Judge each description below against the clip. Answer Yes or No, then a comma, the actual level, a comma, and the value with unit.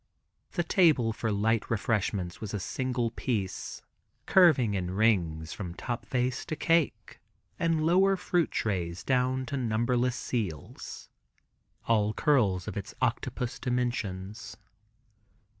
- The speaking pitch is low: Yes, low, 115 Hz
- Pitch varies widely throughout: No, average, 4.4 semitones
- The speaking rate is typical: No, slow, 120 wpm